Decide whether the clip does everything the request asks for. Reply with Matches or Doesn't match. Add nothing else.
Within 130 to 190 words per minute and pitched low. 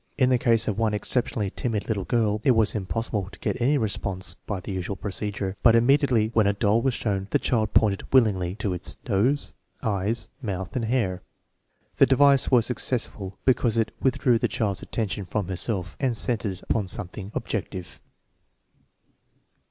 Matches